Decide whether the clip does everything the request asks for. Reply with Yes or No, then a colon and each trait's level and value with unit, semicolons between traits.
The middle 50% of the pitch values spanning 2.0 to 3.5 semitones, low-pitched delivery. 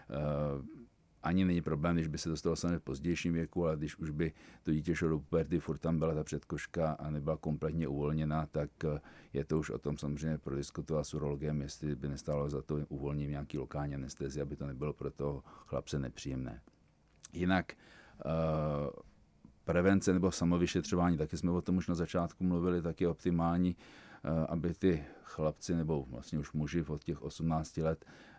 Yes: narrow, 2.6 semitones; very low, 80 Hz